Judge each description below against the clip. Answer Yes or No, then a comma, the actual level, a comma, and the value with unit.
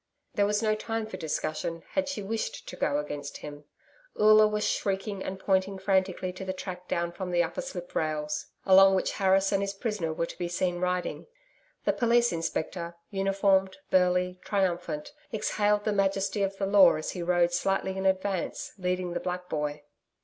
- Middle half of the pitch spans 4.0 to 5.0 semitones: No, narrow, 2.4 semitones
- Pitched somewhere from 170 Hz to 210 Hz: Yes, high, 190 Hz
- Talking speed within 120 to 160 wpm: No, average, 180 wpm